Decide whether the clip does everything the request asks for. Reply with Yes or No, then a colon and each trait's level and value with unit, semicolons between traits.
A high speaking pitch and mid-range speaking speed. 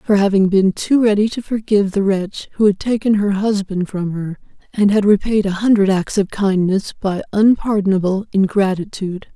Yes: high, 200 Hz; average, 175 wpm